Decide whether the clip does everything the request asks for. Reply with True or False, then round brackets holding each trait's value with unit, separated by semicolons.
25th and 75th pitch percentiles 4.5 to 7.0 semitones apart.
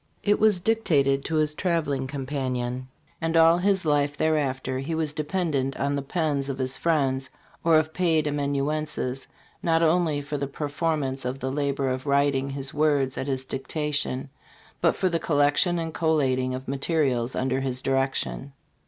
False (3.0 semitones)